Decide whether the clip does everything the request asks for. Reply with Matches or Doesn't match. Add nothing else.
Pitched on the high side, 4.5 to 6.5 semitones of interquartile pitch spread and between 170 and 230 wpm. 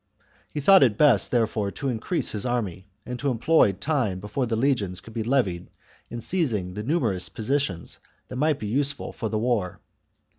Doesn't match